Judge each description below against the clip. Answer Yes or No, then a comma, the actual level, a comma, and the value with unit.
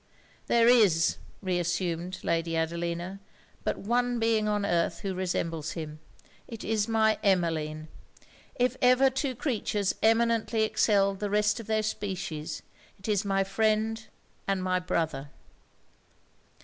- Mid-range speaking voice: No, high, 195 Hz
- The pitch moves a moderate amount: Yes, average, 4.4 semitones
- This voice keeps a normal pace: No, slow, 125 wpm